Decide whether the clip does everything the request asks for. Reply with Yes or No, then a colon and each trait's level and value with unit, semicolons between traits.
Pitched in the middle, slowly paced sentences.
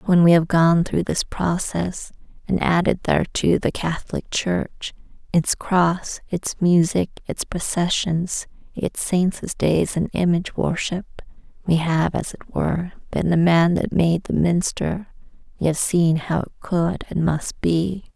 No: medium, 170 Hz; average, 150 wpm